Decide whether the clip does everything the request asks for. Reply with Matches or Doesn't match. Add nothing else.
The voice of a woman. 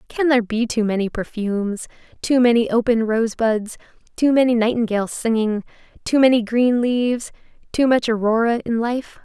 Matches